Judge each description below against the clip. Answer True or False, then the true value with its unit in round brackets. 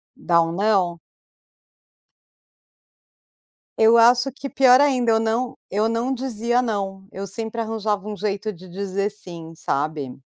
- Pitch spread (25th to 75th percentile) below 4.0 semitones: True (3.5 semitones)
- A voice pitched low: False (215 Hz)